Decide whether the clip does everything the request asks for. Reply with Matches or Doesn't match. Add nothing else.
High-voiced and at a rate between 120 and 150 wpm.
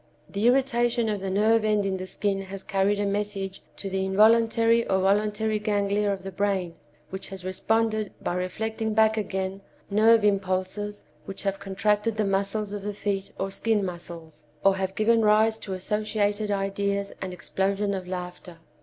Doesn't match